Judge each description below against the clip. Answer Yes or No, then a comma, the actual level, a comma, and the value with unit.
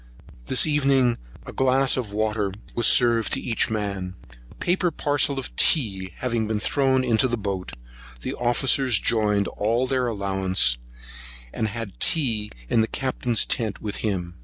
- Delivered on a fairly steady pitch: No, average, 4.1 semitones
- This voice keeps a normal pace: Yes, average, 160 wpm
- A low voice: Yes, low, 115 Hz